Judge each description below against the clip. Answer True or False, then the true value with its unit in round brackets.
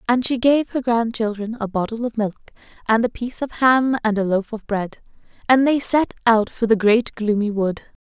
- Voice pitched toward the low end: False (230 Hz)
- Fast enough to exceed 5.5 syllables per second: False (4.9 syllables/s)